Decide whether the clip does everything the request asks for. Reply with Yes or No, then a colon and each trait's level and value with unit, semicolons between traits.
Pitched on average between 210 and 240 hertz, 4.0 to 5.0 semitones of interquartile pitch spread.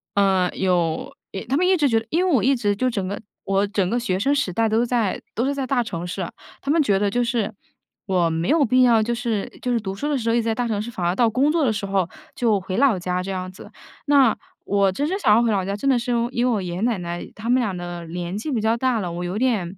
Yes: high, 220 Hz; average, 4.6 semitones